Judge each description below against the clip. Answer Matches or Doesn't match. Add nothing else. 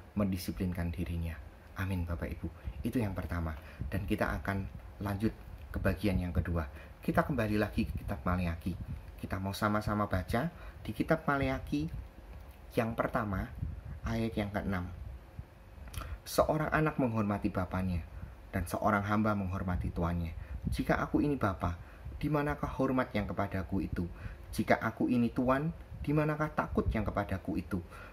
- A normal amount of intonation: Matches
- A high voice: Doesn't match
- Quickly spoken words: Doesn't match